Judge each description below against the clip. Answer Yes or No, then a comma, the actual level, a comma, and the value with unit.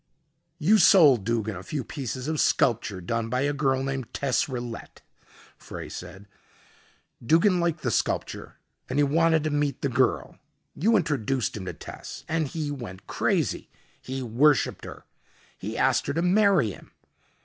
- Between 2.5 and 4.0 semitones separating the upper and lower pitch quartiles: No, average, 5.1 semitones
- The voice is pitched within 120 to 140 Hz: Yes, low, 135 Hz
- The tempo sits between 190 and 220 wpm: No, average, 160 wpm